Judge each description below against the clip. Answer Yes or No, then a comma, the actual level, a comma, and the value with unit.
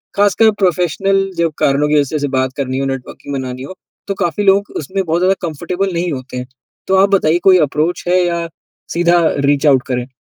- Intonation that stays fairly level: No, average, 5.2 semitones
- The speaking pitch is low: No, medium, 165 Hz